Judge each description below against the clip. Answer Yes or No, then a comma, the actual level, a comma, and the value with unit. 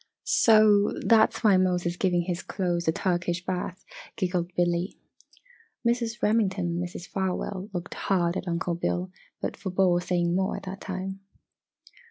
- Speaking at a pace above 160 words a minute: No, average, 150 wpm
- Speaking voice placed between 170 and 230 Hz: Yes, medium, 185 Hz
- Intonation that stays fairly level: Yes, narrow, 1.9 semitones